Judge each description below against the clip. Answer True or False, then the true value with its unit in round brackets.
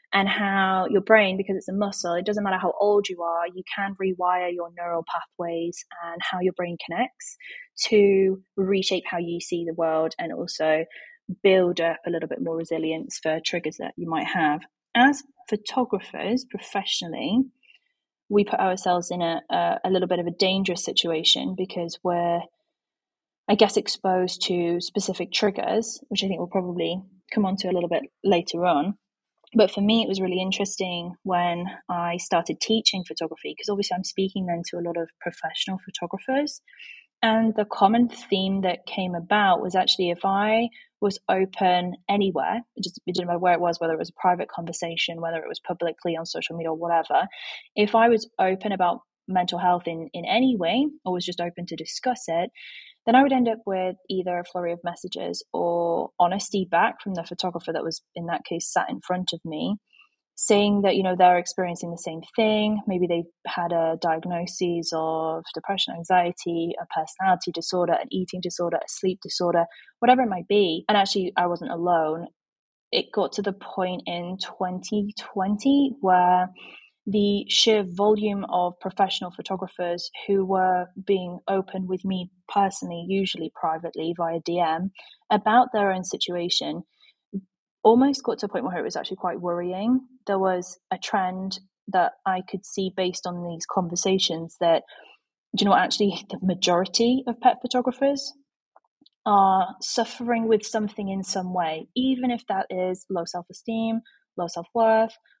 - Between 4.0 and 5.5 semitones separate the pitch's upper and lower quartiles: False (3.3 semitones)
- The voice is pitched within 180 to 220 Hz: True (185 Hz)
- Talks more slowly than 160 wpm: False (175 wpm)